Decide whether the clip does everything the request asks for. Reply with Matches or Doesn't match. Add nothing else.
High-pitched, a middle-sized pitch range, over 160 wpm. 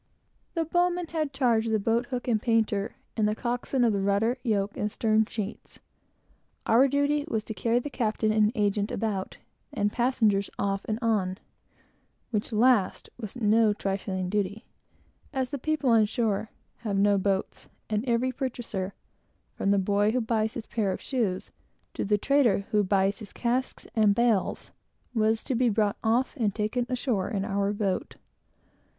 Matches